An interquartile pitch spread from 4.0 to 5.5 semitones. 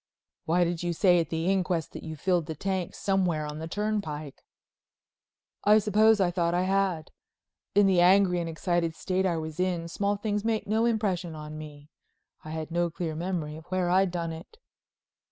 No: average, 3.2 semitones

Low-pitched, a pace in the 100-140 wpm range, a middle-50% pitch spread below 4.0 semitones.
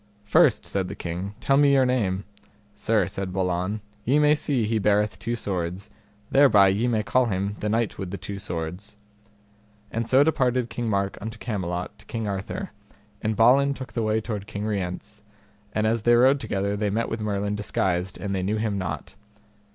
No: low, 105 Hz; average, 190 wpm; average, 3.2 semitones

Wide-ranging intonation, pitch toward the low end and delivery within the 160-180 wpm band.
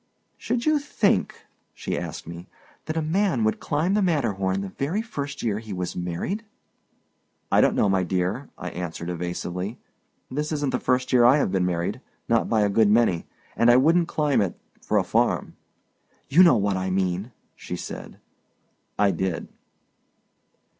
Yes: wide, 8.1 semitones; low, 110 Hz; average, 165 wpm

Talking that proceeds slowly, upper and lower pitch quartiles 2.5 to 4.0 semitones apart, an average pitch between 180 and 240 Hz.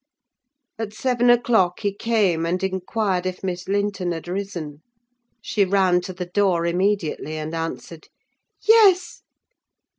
Yes: slow, 125 wpm; average, 2.9 semitones; high, 190 Hz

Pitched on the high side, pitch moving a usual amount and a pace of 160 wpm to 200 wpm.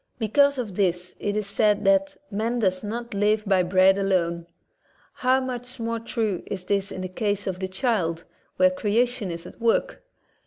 Yes: high, 205 Hz; average, 3.7 semitones; average, 180 wpm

